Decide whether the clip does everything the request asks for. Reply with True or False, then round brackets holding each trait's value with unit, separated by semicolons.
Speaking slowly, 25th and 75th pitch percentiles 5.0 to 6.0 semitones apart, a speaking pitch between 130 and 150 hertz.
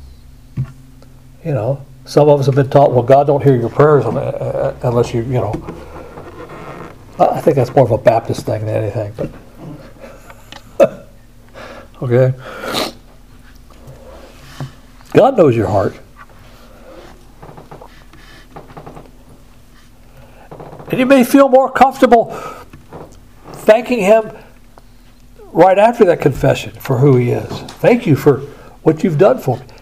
True (115 wpm; 5.3 semitones; 135 Hz)